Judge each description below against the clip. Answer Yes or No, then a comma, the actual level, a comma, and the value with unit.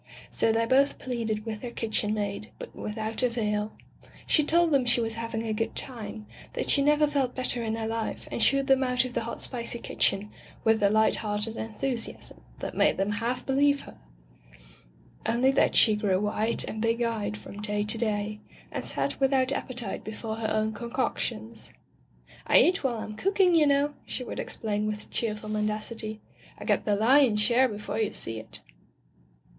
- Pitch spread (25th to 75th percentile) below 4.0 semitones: Yes, average, 3.0 semitones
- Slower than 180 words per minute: No, average, 190 wpm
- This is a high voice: Yes, high, 225 Hz